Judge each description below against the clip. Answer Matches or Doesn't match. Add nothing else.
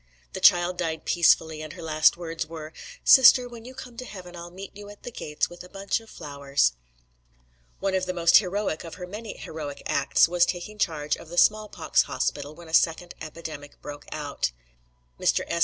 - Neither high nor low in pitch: Matches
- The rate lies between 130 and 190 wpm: Doesn't match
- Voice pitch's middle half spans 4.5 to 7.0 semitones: Doesn't match